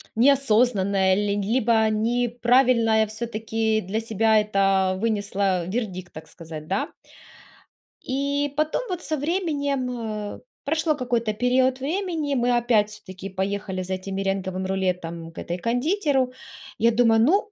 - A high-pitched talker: Yes, high, 225 Hz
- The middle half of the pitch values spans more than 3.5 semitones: Yes, average, 4.8 semitones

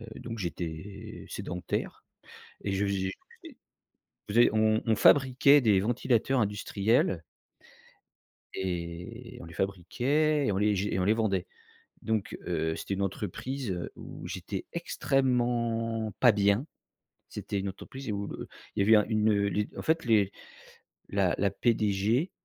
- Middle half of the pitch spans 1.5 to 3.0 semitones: No, average, 3.4 semitones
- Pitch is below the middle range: Yes, low, 105 Hz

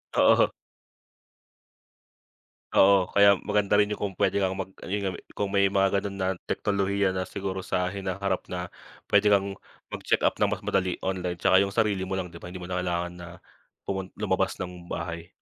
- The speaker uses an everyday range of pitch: No, narrow, 1.6 semitones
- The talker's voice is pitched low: Yes, very low, 95 Hz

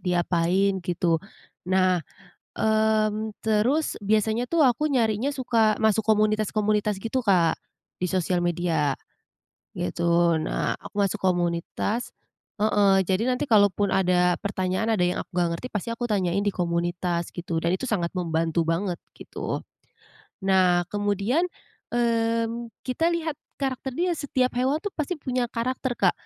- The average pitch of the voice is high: Yes, high, 205 Hz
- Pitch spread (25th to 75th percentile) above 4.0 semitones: Yes, average, 4.6 semitones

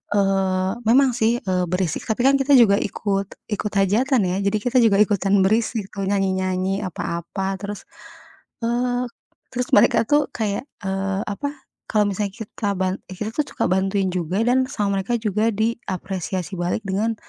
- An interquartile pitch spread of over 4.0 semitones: No, average, 3.1 semitones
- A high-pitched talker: Yes, high, 200 Hz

